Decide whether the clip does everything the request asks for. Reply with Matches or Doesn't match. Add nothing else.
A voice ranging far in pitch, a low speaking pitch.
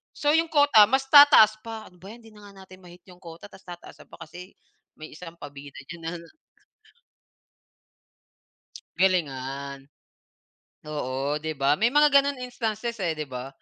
Doesn't match